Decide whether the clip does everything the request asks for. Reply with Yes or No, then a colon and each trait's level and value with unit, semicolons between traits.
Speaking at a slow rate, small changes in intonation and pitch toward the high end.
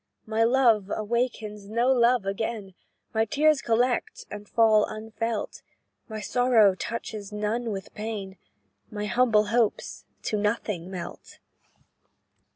Yes: slow, 115 wpm; narrow, 2.1 semitones; high, 220 Hz